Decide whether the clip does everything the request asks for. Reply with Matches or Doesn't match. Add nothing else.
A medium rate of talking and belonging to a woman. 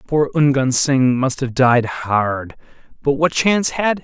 Doesn't match